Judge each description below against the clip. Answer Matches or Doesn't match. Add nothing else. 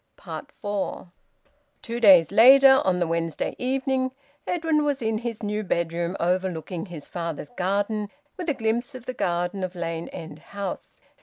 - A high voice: Matches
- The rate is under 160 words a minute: Matches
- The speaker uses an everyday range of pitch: Doesn't match